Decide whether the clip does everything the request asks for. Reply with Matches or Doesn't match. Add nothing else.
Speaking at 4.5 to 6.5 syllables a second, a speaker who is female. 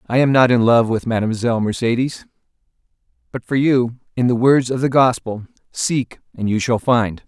Doesn't match